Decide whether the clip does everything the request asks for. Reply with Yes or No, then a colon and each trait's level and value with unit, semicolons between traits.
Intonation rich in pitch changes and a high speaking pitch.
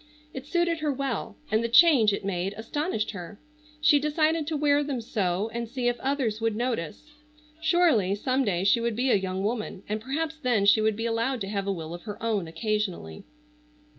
Yes: wide, 5.8 semitones; high, 230 Hz